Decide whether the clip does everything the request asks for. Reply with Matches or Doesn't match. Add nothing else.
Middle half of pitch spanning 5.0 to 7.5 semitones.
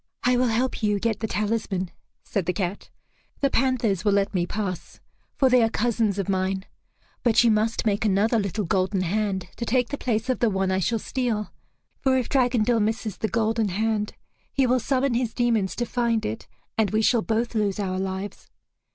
Doesn't match